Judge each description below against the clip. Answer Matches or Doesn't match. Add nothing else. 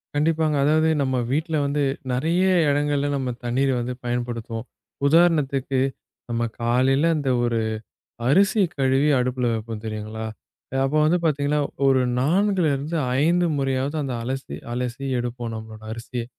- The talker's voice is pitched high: Doesn't match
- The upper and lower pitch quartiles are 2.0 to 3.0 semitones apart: Doesn't match